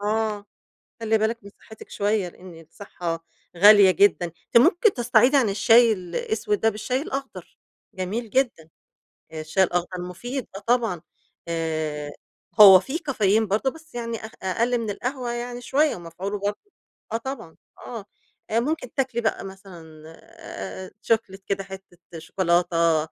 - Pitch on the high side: Yes, high, 210 Hz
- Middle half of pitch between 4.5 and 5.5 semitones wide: Yes, average, 4.8 semitones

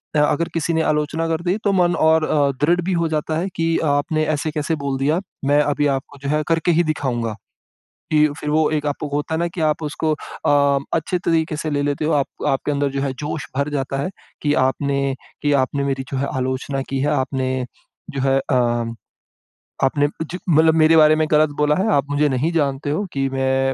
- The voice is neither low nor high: Yes, medium, 150 Hz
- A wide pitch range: No, narrow, 2.4 semitones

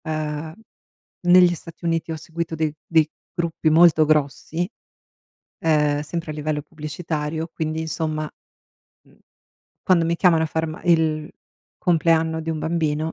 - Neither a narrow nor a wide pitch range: No, narrow, 1.3 semitones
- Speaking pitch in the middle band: Yes, medium, 160 Hz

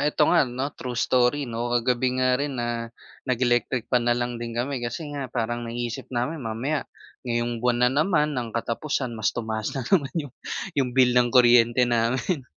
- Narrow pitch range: Yes, narrow, 2.1 semitones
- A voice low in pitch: Yes, low, 125 Hz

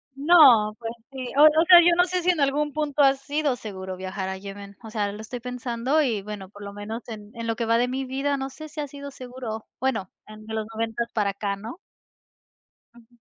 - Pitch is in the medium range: No, high, 235 Hz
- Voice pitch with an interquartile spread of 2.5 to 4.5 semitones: No, average, 5.0 semitones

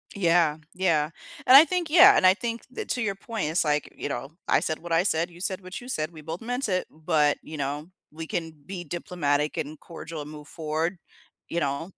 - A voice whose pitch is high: No, medium, 170 Hz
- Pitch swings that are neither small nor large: Yes, average, 4.0 semitones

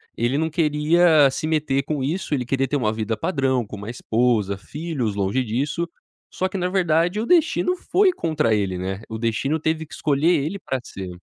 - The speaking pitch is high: No, medium, 140 Hz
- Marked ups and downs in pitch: Yes, wide, 6.0 semitones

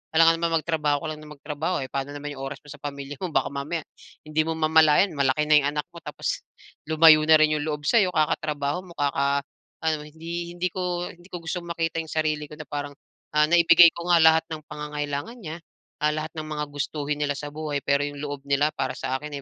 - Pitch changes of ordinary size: No, narrow, 2.1 semitones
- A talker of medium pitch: Yes, medium, 155 Hz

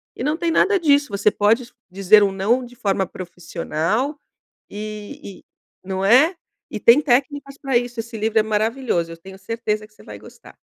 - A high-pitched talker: Yes, high, 220 Hz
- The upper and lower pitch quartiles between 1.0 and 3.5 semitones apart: No, average, 5.0 semitones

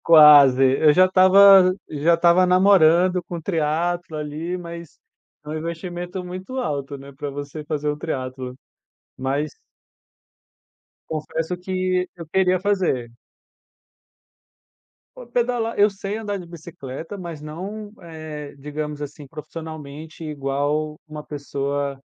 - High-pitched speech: No, medium, 160 Hz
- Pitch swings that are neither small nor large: Yes, average, 3.7 semitones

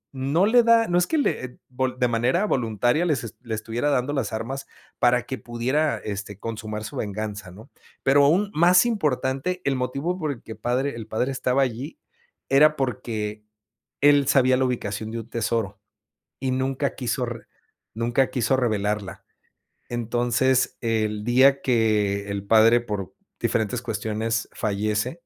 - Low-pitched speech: Yes, low, 120 Hz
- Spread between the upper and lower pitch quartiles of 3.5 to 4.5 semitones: Yes, average, 3.9 semitones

